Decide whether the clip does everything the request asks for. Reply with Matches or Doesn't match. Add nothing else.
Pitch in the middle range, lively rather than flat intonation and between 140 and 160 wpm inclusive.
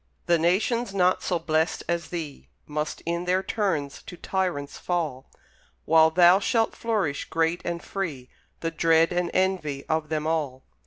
Doesn't match